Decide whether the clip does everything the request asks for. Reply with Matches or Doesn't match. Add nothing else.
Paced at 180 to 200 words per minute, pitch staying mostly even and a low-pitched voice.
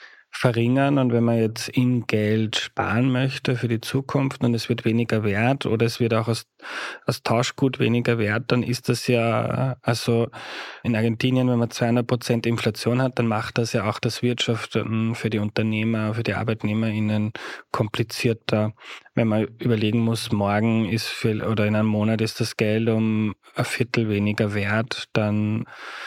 Doesn't match